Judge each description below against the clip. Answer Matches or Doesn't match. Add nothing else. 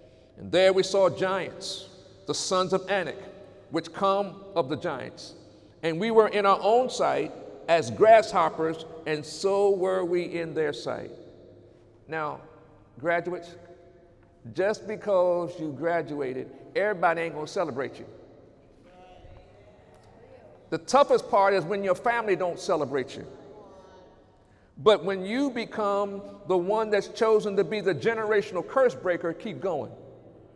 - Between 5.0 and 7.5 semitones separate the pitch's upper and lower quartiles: Doesn't match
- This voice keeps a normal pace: Doesn't match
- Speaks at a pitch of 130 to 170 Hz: Doesn't match